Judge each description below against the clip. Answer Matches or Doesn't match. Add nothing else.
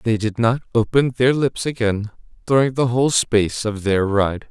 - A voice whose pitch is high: Doesn't match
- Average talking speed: Matches